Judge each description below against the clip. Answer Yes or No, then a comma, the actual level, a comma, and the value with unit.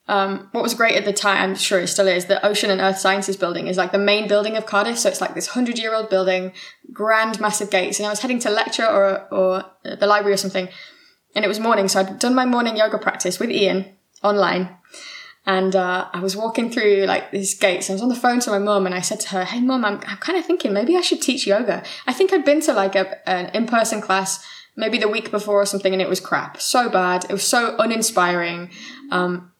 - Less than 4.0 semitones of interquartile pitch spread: Yes, average, 2.9 semitones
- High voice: Yes, high, 200 Hz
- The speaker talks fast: Yes, fast, 250 wpm